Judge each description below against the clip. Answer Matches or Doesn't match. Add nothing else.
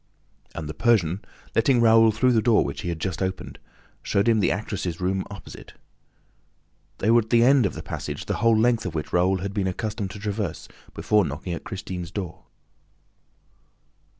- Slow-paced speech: Doesn't match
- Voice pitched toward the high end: Doesn't match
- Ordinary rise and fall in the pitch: Matches